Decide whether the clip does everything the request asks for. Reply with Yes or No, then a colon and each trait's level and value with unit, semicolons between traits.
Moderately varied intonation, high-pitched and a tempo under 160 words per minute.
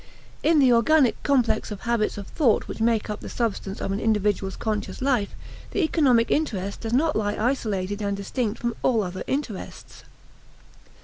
No: average, 4.0 semitones; high, 225 Hz; average, 170 wpm